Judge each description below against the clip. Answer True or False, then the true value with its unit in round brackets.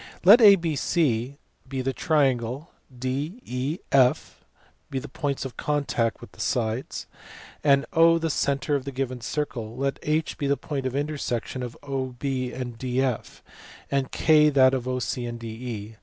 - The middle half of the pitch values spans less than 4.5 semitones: True (2.8 semitones)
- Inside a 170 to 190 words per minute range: False (155 wpm)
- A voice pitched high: False (135 Hz)